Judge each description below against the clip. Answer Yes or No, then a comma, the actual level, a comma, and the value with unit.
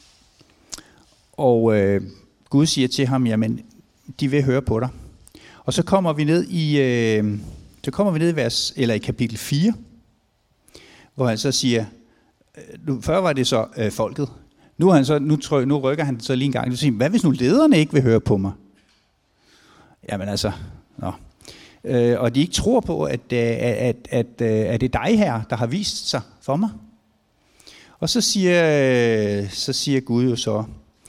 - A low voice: Yes, low, 125 Hz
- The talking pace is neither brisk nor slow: Yes, average, 185 wpm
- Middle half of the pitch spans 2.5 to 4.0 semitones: No, average, 4.8 semitones